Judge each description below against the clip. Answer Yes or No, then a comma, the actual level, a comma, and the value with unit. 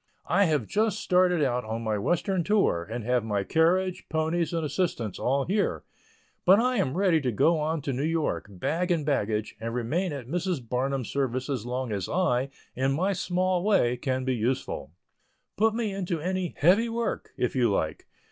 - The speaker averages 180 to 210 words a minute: Yes, average, 185 wpm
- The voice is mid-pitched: Yes, medium, 150 Hz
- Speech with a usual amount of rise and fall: No, wide, 6.7 semitones